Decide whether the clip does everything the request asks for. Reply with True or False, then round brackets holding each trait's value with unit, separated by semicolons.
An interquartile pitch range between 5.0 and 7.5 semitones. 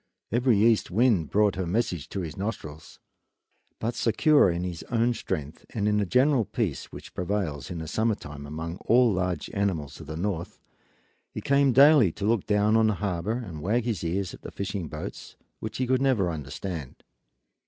True (5.5 semitones)